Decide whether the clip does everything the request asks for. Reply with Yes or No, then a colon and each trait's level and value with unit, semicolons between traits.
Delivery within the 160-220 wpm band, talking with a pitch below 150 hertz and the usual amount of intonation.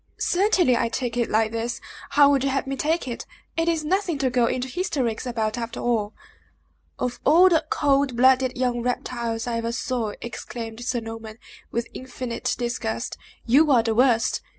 No: average, 175 wpm; high, 245 Hz; average, 3.1 semitones